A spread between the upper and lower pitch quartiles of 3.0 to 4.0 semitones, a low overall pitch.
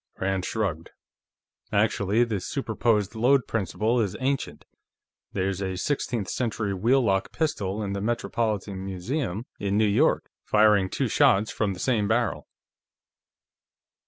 Yes: average, 3.3 semitones; low, 105 Hz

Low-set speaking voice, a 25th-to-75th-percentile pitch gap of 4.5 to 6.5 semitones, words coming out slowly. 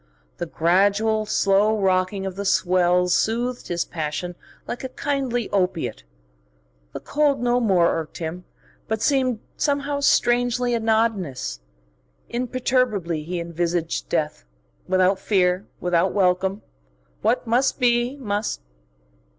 No: high, 200 Hz; average, 5.3 semitones; slow, 115 wpm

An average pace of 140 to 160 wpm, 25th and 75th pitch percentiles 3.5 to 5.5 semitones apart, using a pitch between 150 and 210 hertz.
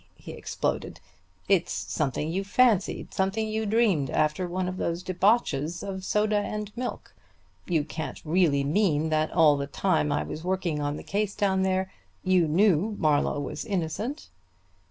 Yes: average, 155 wpm; average, 4.7 semitones; medium, 185 Hz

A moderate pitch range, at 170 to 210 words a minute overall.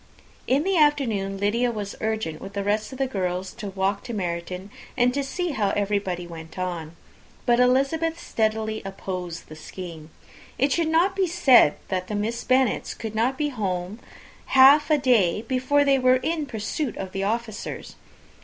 No: wide, 5.7 semitones; average, 175 wpm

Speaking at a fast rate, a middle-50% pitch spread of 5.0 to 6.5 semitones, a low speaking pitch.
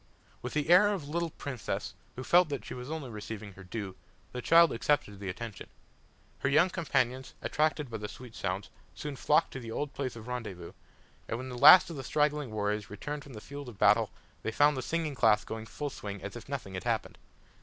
Yes: fast, 220 wpm; wide, 5.5 semitones; low, 125 Hz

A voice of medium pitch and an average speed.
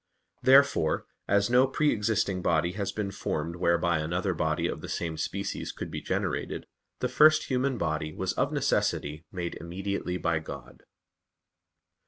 No: very low, 90 Hz; average, 150 wpm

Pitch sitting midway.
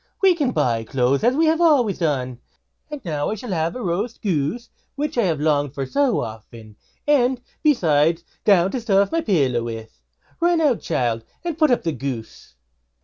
Yes: medium, 180 Hz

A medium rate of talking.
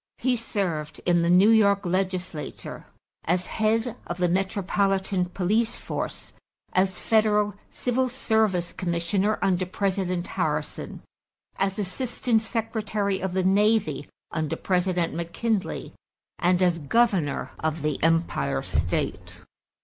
No: slow, 115 wpm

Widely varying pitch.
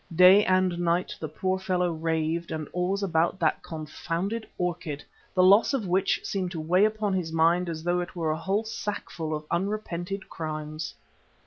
No: average, 2.8 semitones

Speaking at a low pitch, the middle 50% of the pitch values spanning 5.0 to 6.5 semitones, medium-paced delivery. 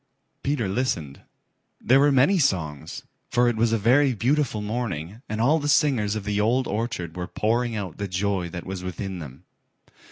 Yes: low, 110 Hz; wide, 5.4 semitones; average, 180 wpm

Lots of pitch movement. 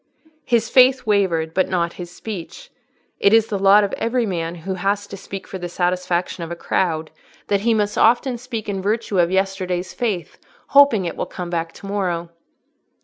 No: average, 3.7 semitones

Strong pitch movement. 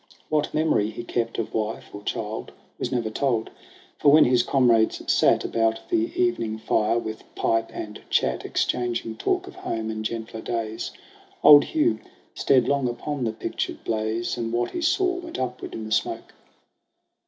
No: average, 3.7 semitones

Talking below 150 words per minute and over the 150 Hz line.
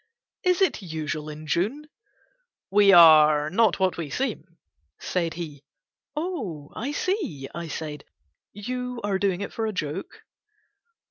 Yes: slow, 135 wpm; medium, 185 Hz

